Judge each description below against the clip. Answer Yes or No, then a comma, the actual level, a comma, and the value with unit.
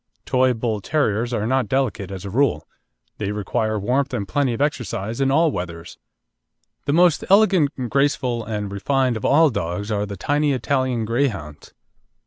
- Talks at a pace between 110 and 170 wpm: Yes, average, 160 wpm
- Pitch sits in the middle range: No, low, 120 Hz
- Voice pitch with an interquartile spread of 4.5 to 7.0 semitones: Yes, average, 5.2 semitones